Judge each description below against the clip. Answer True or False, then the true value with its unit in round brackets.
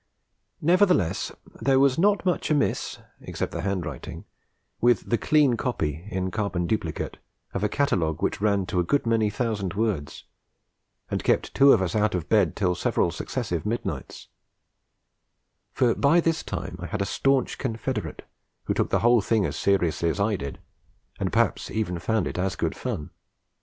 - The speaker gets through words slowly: False (170 wpm)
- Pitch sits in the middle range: False (105 Hz)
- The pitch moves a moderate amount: False (5.9 semitones)